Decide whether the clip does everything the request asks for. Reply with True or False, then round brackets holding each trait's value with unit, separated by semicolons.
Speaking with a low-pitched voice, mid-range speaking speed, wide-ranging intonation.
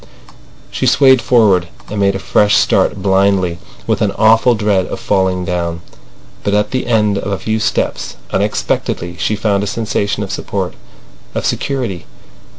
False (100 Hz; 155 wpm; 2.6 semitones)